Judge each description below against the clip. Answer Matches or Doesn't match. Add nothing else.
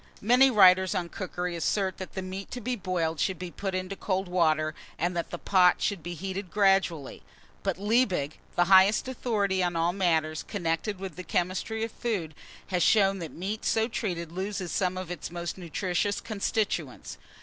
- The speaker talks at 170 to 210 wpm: Matches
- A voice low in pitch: Doesn't match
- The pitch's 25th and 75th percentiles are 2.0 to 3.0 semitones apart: Matches